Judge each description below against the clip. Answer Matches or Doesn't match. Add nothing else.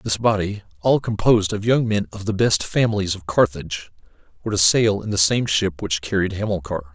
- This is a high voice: Doesn't match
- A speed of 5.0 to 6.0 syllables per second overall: Matches